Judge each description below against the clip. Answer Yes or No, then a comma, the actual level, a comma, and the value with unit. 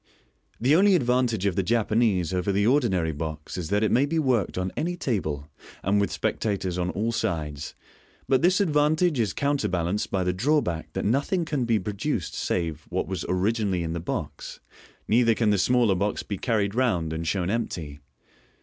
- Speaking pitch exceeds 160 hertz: No, low, 105 Hz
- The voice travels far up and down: Yes, wide, 5.8 semitones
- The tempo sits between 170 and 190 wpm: Yes, average, 180 wpm